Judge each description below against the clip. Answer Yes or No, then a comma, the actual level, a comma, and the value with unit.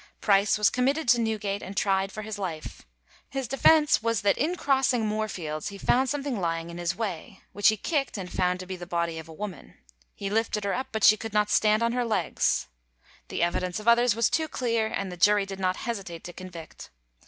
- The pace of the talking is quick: Yes, fast, 220 wpm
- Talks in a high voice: Yes, high, 210 Hz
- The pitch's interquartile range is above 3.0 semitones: Yes, average, 4.1 semitones